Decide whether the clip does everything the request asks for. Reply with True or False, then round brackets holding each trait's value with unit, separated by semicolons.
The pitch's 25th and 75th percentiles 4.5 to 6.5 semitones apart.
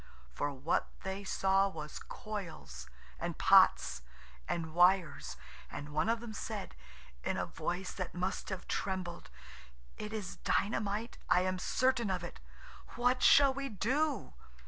False (4.1 semitones)